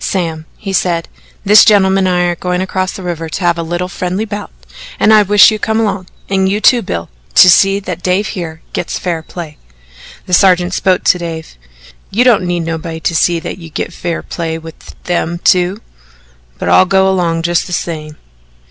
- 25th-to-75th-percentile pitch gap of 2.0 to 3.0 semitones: Yes, narrow, 2.5 semitones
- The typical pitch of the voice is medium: Yes, medium, 180 Hz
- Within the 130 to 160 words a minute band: No, average, 200 wpm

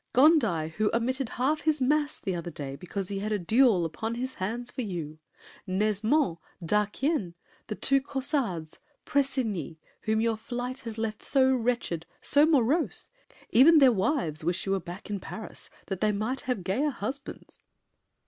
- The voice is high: Yes, high, 225 Hz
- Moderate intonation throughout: No, wide, 5.9 semitones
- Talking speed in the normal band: Yes, average, 160 wpm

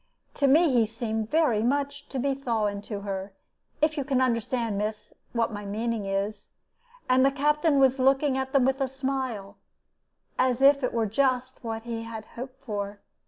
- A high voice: Yes, very high, 250 Hz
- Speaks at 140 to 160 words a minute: No, average, 180 wpm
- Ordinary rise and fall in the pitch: Yes, average, 3.9 semitones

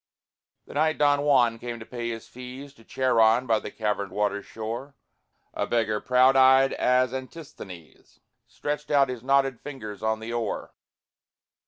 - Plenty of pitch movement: No, average, 3.3 semitones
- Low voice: Yes, low, 125 Hz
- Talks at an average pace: Yes, average, 155 wpm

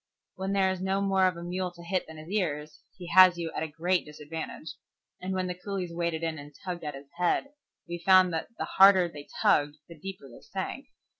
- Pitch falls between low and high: Yes, medium, 175 Hz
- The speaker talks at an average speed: No, fast, 225 wpm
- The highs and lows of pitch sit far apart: No, average, 2.8 semitones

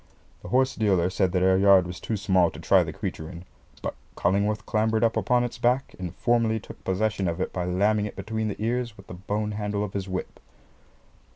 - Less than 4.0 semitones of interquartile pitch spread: Yes, average, 2.8 semitones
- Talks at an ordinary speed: No, fast, 215 wpm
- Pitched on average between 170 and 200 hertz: No, low, 100 Hz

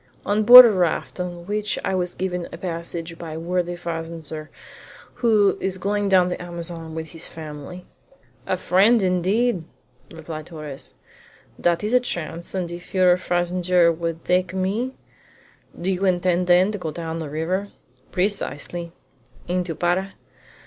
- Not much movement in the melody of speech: Yes, narrow, 2.2 semitones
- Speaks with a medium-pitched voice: Yes, medium, 180 Hz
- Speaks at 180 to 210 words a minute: No, average, 155 wpm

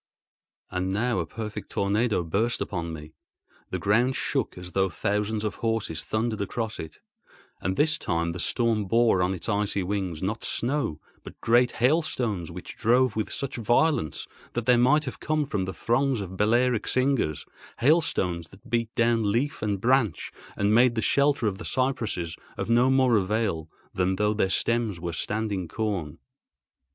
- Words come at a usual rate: Yes, average, 165 wpm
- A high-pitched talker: No, low, 110 Hz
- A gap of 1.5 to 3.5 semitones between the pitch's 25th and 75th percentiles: No, average, 4.3 semitones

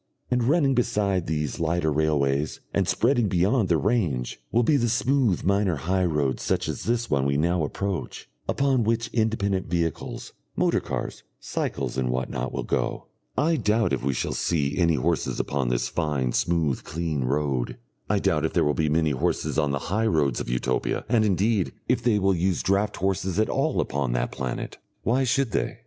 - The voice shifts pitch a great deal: Yes, wide, 7.4 semitones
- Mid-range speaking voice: No, very low, 85 Hz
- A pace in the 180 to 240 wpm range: Yes, average, 190 wpm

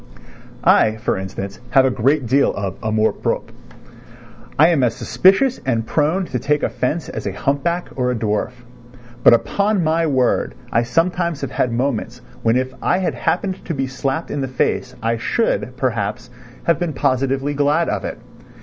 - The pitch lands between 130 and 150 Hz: Yes, low, 135 Hz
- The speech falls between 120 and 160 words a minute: No, average, 175 wpm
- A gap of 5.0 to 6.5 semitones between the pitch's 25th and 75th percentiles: Yes, wide, 5.4 semitones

